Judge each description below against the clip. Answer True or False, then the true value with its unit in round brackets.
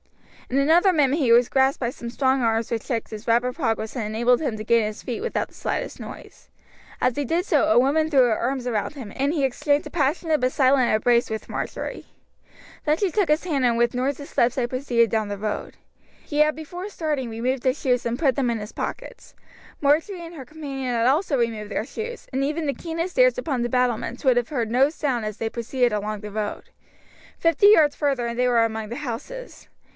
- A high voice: True (255 Hz)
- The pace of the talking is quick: True (220 wpm)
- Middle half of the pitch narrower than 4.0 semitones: False (4.3 semitones)